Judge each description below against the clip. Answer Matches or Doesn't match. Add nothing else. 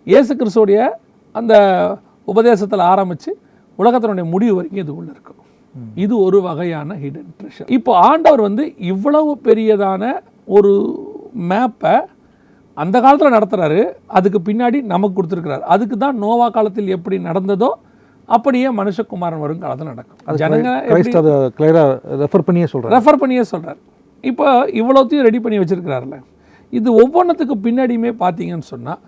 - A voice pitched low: Doesn't match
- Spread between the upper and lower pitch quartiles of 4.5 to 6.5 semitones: Matches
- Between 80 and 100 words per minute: Doesn't match